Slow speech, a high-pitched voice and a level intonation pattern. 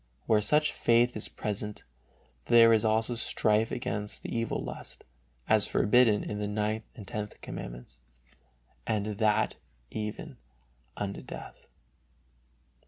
No: slow, 120 wpm; low, 110 Hz; narrow, 1.7 semitones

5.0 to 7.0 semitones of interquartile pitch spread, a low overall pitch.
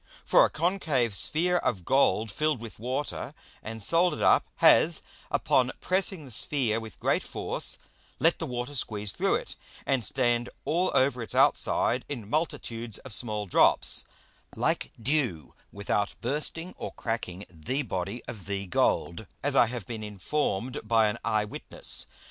Yes: wide, 5.4 semitones; low, 120 Hz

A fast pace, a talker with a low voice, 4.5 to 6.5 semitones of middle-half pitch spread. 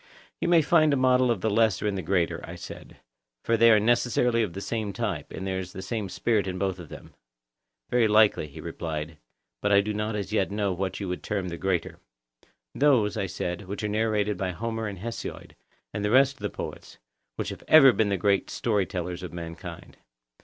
No: fast, 215 wpm; low, 105 Hz; average, 3.3 semitones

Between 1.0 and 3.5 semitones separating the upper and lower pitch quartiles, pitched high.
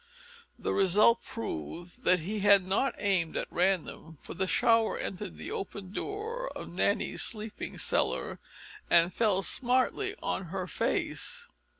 No: average, 4.1 semitones; high, 195 Hz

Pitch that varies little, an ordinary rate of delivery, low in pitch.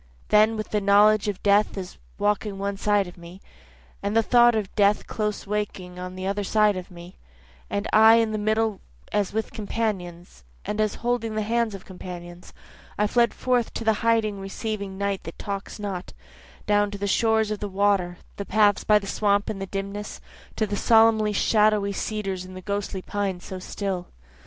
No: narrow, 1.8 semitones; average, 185 wpm; high, 205 Hz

